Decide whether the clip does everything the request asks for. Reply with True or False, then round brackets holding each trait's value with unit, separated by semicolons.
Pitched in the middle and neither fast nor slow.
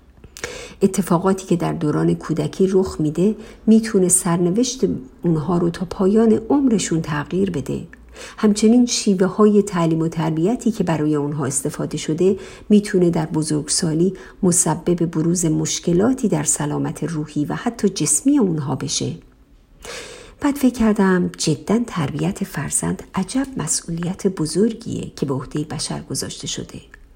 True (175 Hz; 125 wpm)